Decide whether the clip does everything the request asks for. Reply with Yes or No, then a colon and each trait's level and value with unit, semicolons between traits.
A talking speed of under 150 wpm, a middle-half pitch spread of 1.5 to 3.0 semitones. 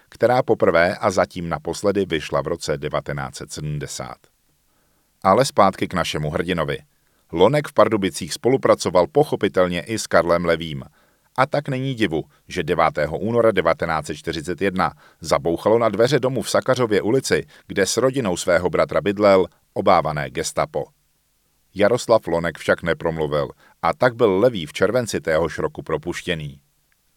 No: average, 130 wpm; average, 4.2 semitones